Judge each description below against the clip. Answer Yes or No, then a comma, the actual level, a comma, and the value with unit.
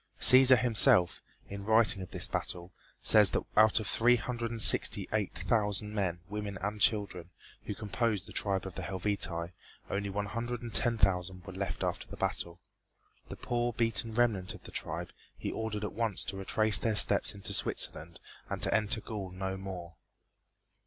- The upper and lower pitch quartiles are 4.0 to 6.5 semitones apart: No, average, 2.8 semitones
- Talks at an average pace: Yes, average, 180 wpm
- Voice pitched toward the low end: Yes, low, 105 Hz